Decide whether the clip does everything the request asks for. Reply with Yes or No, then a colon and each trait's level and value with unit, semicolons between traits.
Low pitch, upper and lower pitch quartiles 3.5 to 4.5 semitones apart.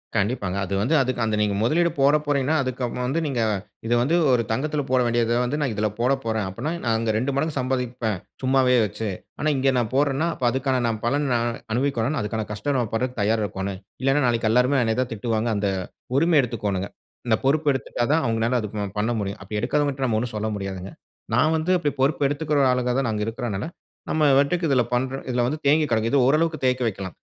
Yes: low, 125 Hz; average, 3.9 semitones